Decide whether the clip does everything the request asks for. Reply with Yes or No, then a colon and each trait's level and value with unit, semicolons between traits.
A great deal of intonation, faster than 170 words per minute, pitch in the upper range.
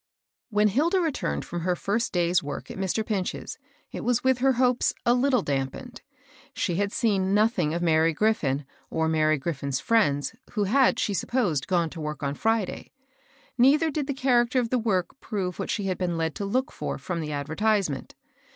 Yes: wide, 6.8 semitones; average, 195 wpm; high, 195 Hz